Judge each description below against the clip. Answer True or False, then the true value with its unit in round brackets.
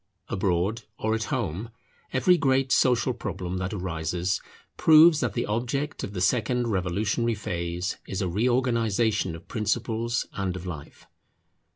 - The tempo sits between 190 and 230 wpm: False (140 wpm)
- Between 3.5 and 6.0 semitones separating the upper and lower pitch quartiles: True (4.8 semitones)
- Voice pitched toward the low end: True (105 Hz)